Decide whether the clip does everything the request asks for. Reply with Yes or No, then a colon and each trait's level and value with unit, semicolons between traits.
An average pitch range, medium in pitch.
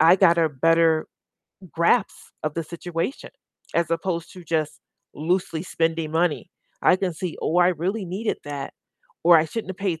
No: narrow, 2.2 semitones; medium, 170 Hz